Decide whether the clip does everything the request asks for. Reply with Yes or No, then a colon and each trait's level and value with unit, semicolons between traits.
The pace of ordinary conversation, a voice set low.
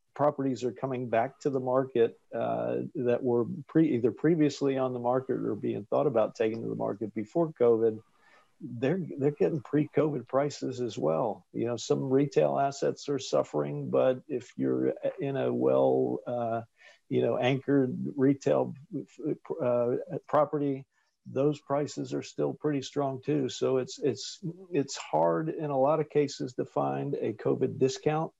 Yes: average, 160 wpm; low, 130 Hz